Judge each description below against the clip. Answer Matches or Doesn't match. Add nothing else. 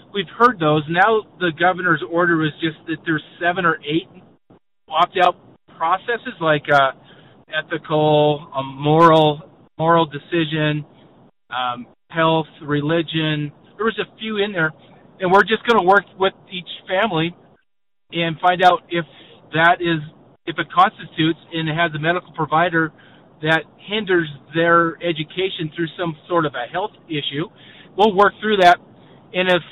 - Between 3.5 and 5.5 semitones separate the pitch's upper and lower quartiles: Doesn't match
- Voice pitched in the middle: Matches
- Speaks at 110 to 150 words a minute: Matches